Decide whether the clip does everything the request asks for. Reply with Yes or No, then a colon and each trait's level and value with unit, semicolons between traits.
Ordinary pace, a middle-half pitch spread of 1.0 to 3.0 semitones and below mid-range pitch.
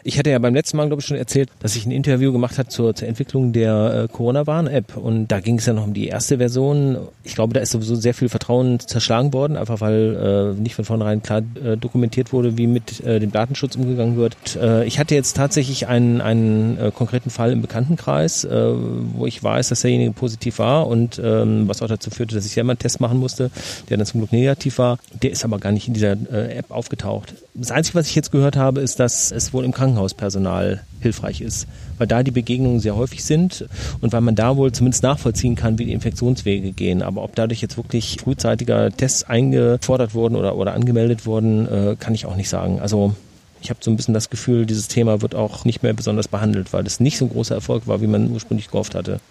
No: fast, 230 wpm; average, 2.7 semitones; low, 115 Hz